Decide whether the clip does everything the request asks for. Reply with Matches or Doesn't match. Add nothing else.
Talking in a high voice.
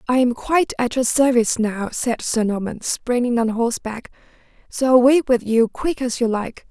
Matches